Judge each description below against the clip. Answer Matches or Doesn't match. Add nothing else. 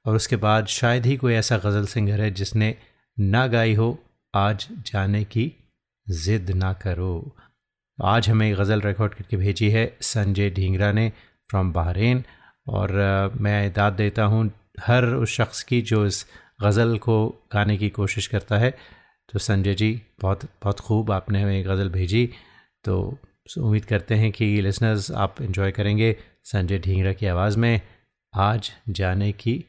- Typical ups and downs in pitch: Doesn't match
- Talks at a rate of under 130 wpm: Doesn't match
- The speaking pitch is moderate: Doesn't match